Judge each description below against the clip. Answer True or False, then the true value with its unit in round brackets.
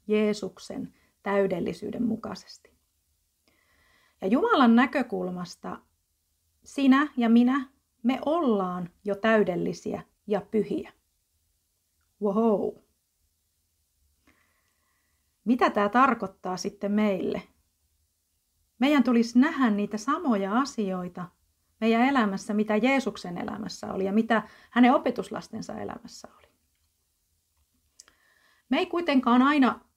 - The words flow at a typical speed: False (85 wpm)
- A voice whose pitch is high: True (205 Hz)